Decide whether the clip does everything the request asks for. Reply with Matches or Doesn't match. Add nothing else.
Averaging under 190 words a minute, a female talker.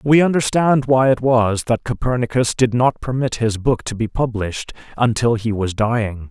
Doesn't match